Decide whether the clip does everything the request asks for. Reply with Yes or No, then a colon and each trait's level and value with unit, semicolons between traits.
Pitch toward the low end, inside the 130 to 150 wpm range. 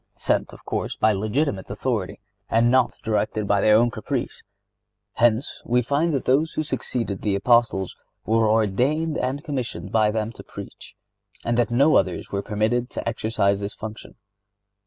No: low, 115 Hz; average, 165 wpm